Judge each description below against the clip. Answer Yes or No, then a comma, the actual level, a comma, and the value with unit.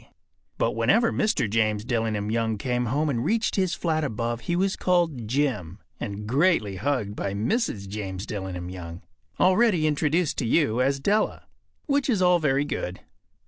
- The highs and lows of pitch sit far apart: Yes, wide, 8.5 semitones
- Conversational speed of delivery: Yes, average, 160 wpm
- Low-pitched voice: Yes, low, 125 Hz